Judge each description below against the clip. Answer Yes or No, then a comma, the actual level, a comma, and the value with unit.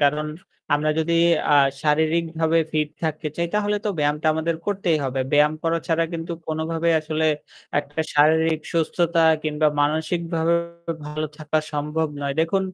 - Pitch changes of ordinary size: No, narrow, 1.7 semitones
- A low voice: No, medium, 160 Hz